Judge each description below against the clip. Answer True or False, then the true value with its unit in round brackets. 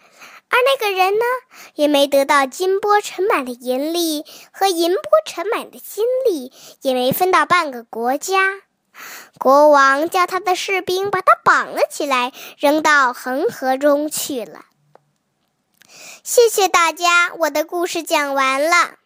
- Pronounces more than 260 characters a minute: False (200 characters per minute)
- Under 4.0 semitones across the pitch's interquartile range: False (4.9 semitones)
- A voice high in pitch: True (335 Hz)